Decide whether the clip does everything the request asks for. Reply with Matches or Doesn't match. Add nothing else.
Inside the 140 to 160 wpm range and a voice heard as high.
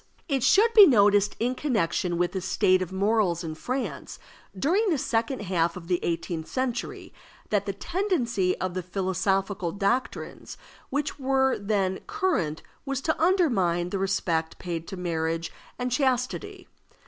Matches